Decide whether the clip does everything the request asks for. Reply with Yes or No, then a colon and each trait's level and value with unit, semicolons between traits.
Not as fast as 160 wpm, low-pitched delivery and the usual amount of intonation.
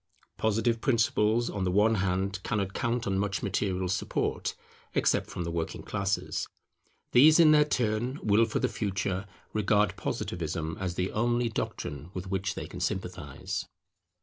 Yes: average, 150 wpm; low, 100 Hz; average, 3.5 semitones